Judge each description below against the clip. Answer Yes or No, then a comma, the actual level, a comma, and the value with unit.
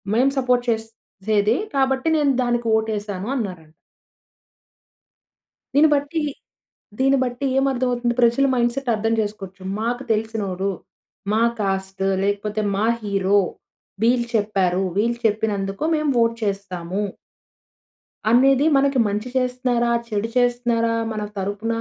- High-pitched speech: Yes, high, 225 Hz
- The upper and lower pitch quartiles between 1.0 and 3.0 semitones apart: No, average, 3.5 semitones